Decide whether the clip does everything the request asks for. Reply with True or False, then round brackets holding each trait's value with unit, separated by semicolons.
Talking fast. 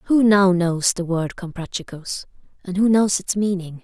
False (170 wpm)